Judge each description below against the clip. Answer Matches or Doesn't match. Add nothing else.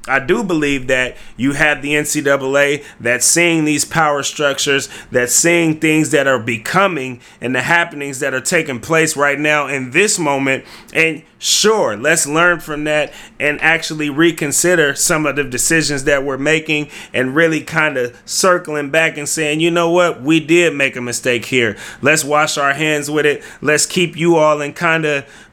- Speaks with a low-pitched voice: Doesn't match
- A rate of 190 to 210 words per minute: Doesn't match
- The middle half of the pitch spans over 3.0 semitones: Doesn't match